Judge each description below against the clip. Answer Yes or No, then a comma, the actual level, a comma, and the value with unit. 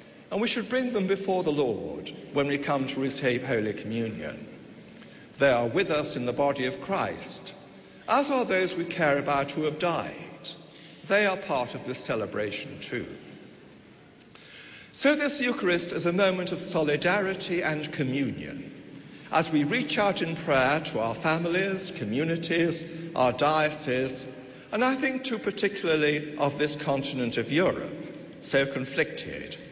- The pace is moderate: Yes, average, 150 wpm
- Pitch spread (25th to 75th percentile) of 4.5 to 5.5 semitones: Yes, average, 5.1 semitones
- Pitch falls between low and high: Yes, medium, 160 Hz